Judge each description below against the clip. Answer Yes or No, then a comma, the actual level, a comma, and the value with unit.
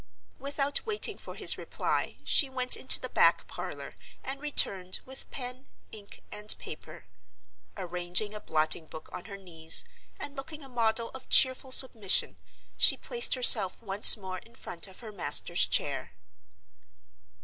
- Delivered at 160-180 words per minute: No, average, 150 wpm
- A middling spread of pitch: No, wide, 6.1 semitones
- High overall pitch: Yes, high, 220 Hz